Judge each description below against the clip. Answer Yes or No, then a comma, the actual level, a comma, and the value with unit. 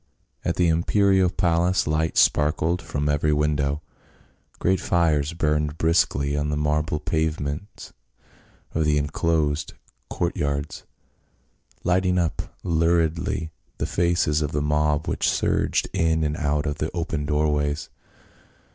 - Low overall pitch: Yes, very low, 75 Hz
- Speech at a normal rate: No, slow, 125 wpm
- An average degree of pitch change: No, narrow, 2.3 semitones